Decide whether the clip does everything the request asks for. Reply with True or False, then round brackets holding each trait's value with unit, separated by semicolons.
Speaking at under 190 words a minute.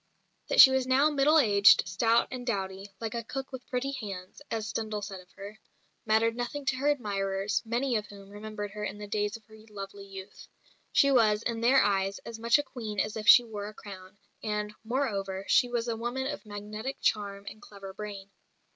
False (205 wpm)